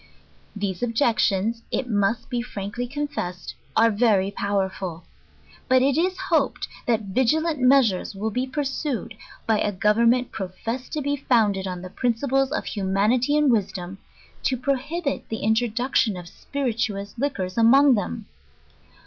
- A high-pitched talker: Yes, high, 230 Hz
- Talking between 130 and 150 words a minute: Yes, average, 140 wpm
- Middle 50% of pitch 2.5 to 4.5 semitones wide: No, average, 5.0 semitones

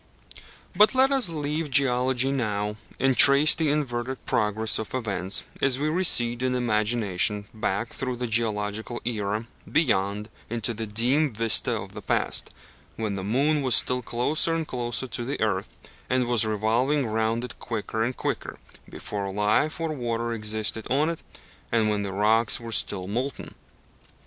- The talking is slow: No, average, 160 wpm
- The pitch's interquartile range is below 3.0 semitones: No, average, 3.8 semitones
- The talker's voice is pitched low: Yes, low, 120 Hz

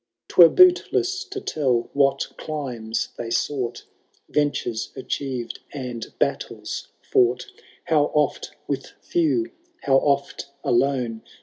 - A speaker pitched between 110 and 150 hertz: Yes, medium, 140 Hz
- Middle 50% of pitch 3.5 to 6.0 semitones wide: Yes, average, 4.2 semitones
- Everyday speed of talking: No, slow, 105 wpm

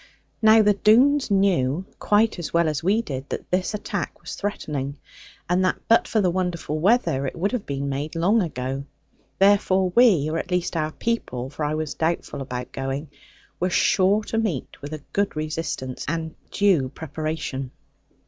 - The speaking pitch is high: No, medium, 170 Hz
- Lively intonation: Yes, wide, 5.7 semitones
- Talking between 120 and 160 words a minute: No, average, 175 wpm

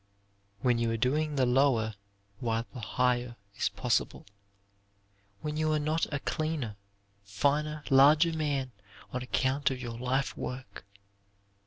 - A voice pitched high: No, low, 130 Hz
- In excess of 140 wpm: No, slow, 135 wpm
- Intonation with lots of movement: No, average, 3.9 semitones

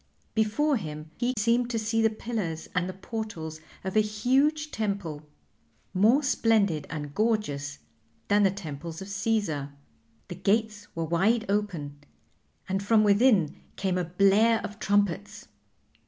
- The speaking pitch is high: Yes, high, 205 Hz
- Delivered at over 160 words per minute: No, average, 140 wpm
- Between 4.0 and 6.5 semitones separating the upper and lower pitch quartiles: Yes, average, 4.6 semitones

